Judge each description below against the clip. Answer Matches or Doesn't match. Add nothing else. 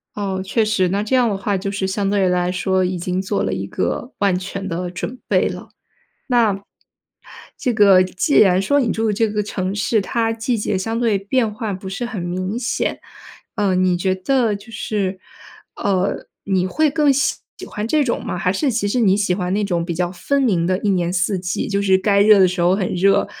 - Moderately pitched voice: Doesn't match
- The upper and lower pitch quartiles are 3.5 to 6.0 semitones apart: Doesn't match